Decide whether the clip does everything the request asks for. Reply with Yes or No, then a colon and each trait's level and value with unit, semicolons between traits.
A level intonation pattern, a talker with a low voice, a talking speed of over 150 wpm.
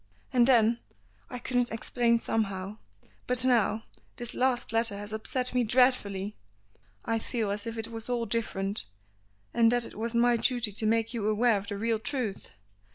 No: narrow, 2.2 semitones; high, 230 Hz; average, 170 wpm